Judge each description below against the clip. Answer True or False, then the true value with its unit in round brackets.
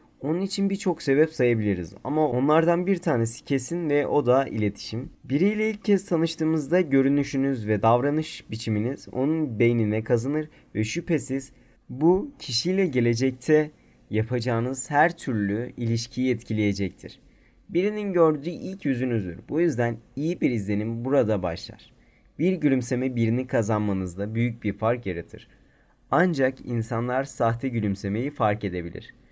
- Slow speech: False (125 wpm)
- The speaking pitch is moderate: False (130 Hz)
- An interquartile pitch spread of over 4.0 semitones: True (5.4 semitones)